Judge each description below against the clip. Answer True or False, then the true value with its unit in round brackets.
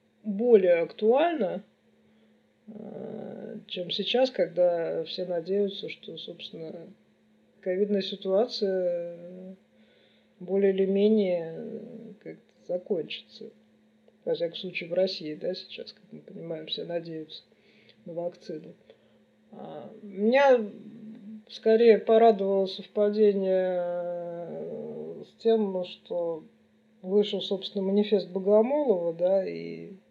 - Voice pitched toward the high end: True (200 Hz)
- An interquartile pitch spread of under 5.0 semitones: True (3.6 semitones)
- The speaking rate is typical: False (85 wpm)